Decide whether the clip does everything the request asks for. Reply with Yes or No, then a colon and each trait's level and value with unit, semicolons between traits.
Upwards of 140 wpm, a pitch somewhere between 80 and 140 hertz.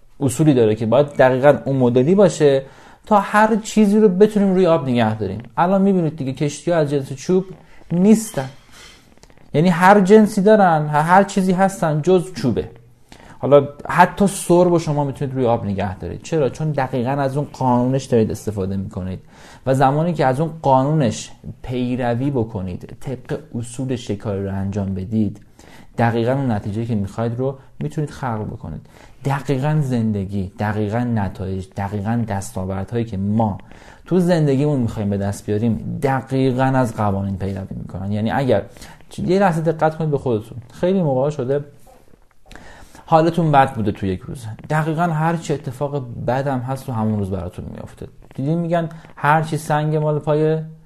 Yes: fast, 155 wpm; low, 135 Hz